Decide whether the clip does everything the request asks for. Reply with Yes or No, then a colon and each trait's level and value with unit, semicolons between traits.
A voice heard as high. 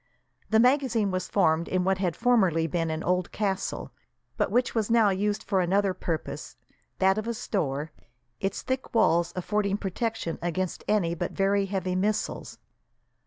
Yes: high, 195 Hz